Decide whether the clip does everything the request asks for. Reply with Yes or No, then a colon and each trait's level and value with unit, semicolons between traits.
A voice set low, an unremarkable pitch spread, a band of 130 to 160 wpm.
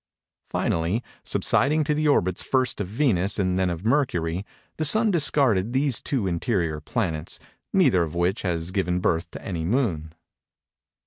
No: very low, 95 Hz; wide, 7.4 semitones; average, 150 wpm